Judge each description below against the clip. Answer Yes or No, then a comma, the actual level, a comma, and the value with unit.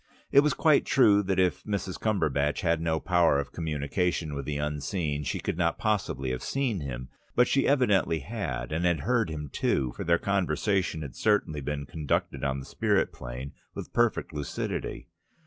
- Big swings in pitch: Yes, wide, 5.9 semitones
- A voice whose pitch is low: Yes, very low, 80 Hz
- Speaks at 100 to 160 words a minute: No, average, 180 wpm